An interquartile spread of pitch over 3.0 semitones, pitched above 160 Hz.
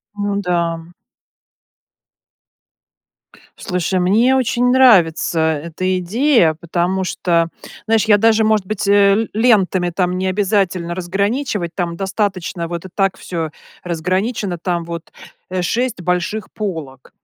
Yes: average, 3.6 semitones; medium, 185 Hz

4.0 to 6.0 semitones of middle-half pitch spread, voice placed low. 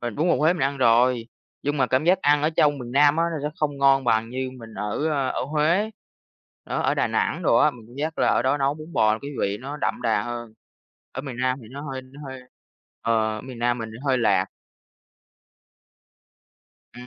No: average, 3.6 semitones; low, 130 Hz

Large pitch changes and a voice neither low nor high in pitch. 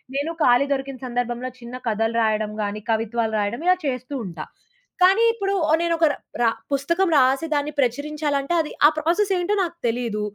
No: wide, 5.9 semitones; very high, 270 Hz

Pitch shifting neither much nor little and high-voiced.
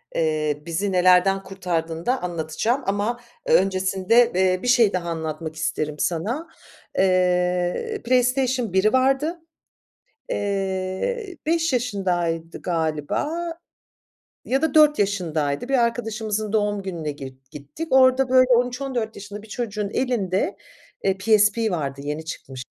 No: wide, 6.3 semitones; high, 195 Hz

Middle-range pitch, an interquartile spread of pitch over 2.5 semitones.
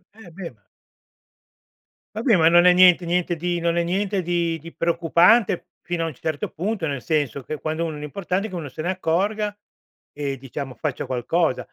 Yes: medium, 170 Hz; average, 2.9 semitones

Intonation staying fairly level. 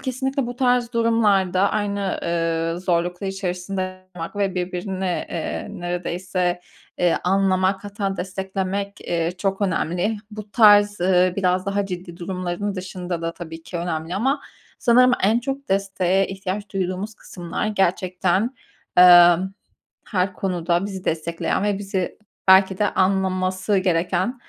Yes: narrow, 2.2 semitones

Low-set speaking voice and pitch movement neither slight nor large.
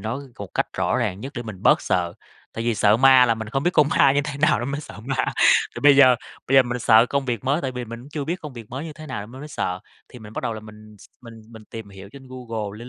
Yes: low, 120 Hz; average, 4.0 semitones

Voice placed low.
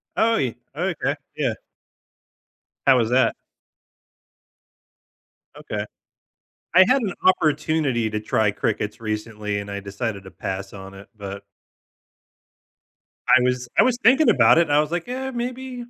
Yes: low, 125 Hz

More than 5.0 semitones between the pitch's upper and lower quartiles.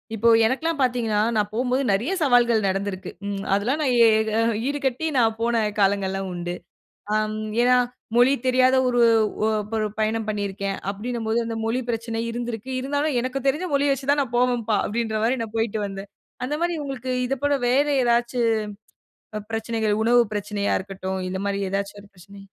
No: average, 3.7 semitones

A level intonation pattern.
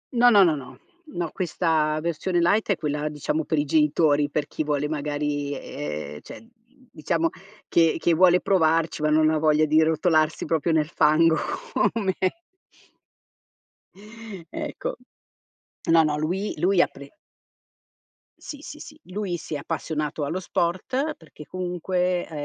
No: average, 3.0 semitones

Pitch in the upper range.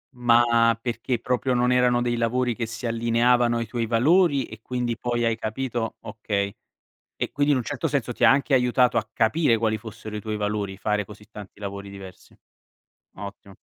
No: low, 115 Hz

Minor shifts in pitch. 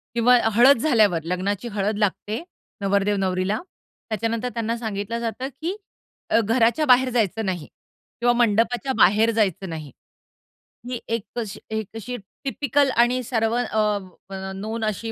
No: average, 3.2 semitones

